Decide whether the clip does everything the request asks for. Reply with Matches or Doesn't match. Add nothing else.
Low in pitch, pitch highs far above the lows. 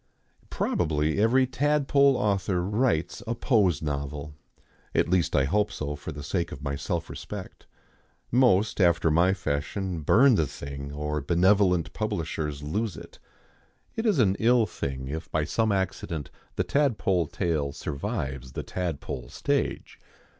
Matches